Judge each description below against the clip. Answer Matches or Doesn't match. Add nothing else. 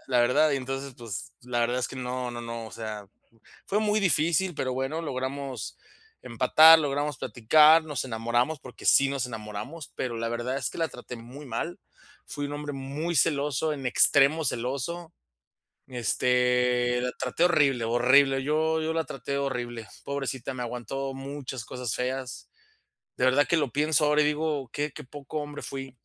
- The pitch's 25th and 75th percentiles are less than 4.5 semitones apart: Matches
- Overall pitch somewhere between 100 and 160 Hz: Matches